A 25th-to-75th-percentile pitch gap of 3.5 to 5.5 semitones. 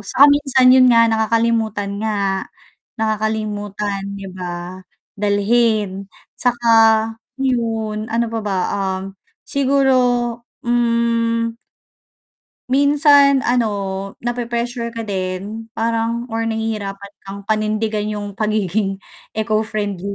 No: narrow, 2.6 semitones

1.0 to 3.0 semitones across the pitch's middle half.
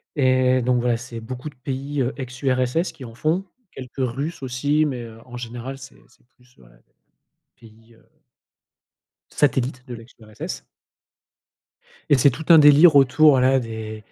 Yes: narrow, 2.6 semitones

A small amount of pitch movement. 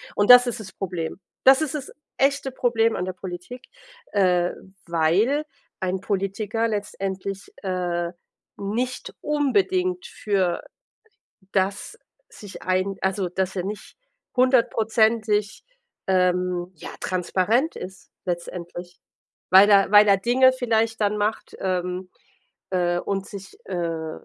No: average, 3.9 semitones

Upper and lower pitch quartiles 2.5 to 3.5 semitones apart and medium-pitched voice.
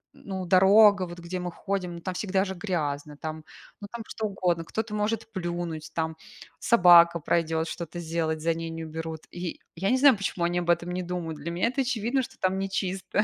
Yes: average, 3.0 semitones; medium, 175 Hz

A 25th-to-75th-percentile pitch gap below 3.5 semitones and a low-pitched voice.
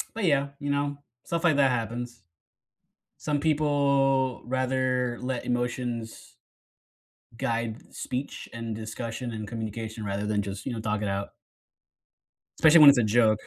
No: average, 3.9 semitones; low, 120 Hz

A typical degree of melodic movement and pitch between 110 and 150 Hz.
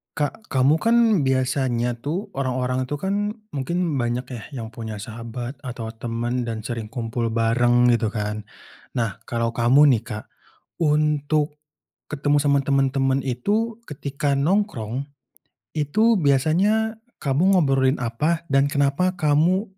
Yes: average, 4.2 semitones; low, 135 Hz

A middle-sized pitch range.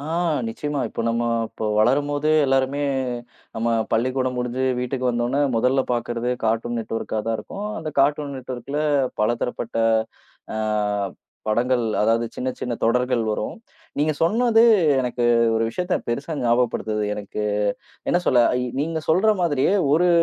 Yes: average, 3.7 semitones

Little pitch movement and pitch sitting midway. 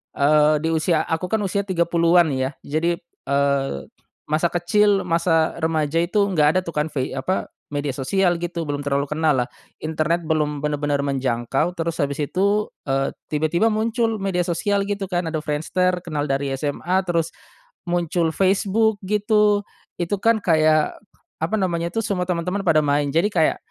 No: average, 3.9 semitones; medium, 165 Hz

